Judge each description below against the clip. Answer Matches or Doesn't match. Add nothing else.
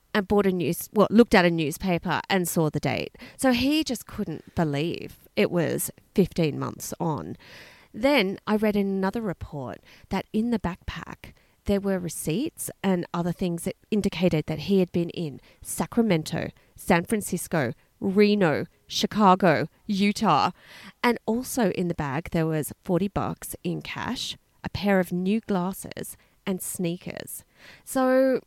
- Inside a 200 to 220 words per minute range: Doesn't match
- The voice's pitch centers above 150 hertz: Matches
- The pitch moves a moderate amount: Matches